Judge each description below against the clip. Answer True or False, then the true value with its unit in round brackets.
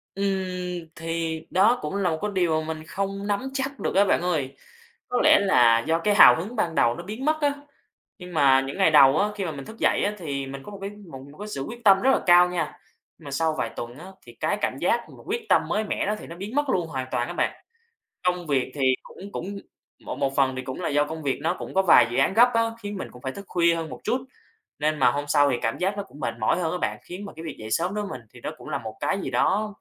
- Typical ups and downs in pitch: False (5.7 semitones)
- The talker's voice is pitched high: False (175 Hz)